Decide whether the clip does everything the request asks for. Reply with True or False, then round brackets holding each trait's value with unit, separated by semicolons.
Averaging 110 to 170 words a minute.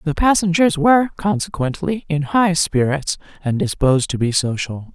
True (145 wpm)